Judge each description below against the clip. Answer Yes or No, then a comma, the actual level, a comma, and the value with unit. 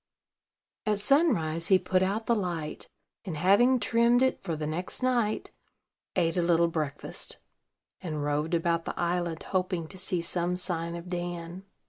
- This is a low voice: No, medium, 175 Hz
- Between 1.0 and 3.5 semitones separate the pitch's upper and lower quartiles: Yes, average, 2.9 semitones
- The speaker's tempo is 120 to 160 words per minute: Yes, average, 155 wpm